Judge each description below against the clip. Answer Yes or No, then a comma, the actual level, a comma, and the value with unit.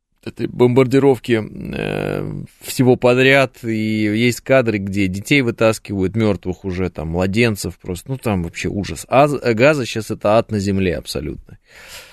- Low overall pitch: Yes, low, 110 Hz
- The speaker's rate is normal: Yes, average, 140 wpm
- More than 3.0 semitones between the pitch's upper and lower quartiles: Yes, average, 4.0 semitones